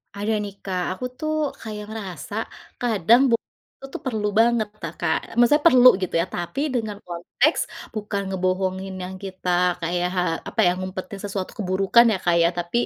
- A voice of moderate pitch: No, high, 195 Hz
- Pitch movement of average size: Yes, average, 3.7 semitones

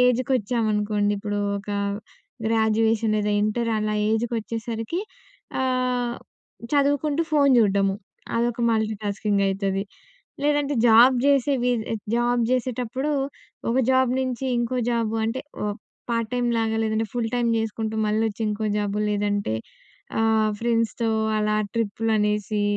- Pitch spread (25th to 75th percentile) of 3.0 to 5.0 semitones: No, narrow, 2.6 semitones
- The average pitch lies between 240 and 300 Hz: No, high, 225 Hz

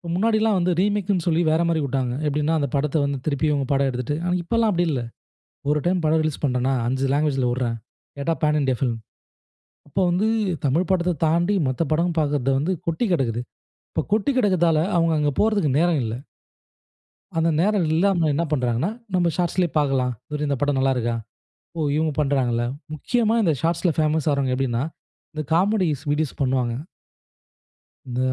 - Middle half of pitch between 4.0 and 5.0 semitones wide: Yes, average, 4.6 semitones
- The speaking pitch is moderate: Yes, medium, 155 Hz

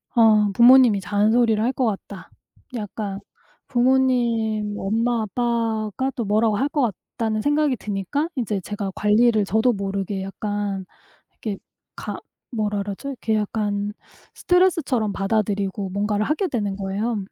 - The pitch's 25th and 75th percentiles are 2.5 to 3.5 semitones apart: Yes, average, 2.9 semitones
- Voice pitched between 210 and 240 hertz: Yes, high, 215 Hz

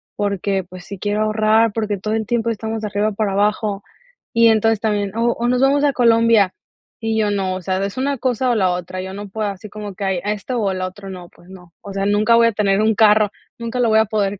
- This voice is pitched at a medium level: No, high, 210 Hz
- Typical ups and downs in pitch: No, narrow, 2.3 semitones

